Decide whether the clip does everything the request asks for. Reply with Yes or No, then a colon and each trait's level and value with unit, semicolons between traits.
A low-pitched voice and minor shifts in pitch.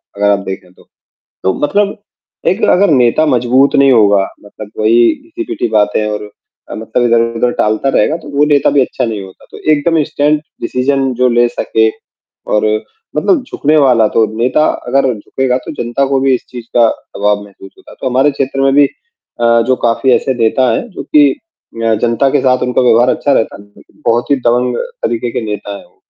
No: low, 125 Hz; average, 3.8 semitones